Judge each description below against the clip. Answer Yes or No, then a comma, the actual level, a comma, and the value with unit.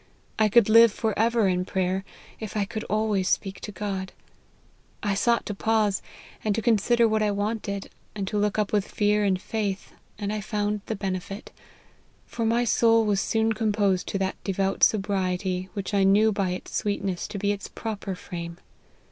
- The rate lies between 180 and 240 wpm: Yes, average, 185 wpm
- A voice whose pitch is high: Yes, high, 205 Hz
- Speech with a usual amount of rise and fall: No, narrow, 2.0 semitones